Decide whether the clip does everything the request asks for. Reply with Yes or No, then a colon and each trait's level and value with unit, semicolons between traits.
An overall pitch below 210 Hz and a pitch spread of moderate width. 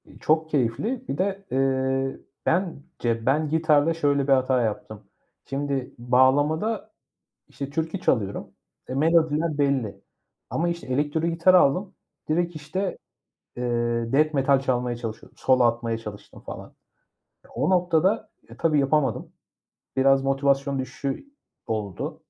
Yes: medium, 140 Hz; average, 3.8 semitones